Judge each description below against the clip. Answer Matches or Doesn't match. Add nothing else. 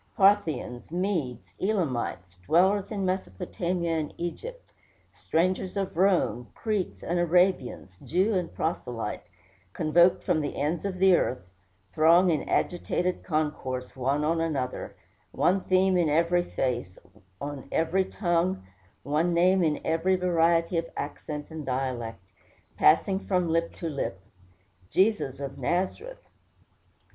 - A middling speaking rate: Doesn't match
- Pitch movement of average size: Matches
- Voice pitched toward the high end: Doesn't match